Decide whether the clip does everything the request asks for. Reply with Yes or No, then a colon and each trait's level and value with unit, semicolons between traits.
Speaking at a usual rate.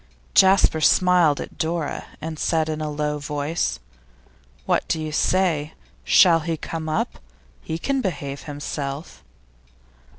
No: slow, 130 wpm